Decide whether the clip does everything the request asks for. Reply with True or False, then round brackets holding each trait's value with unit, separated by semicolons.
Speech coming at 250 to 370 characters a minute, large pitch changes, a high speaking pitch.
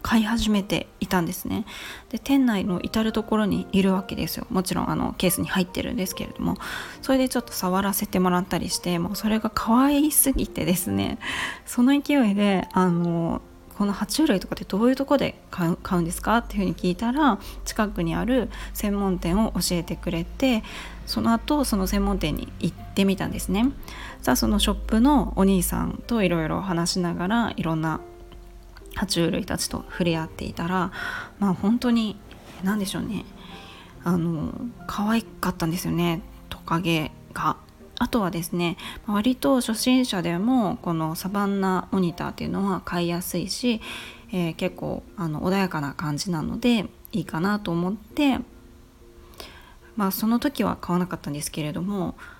False (340 characters per minute; 4.8 semitones; 195 Hz)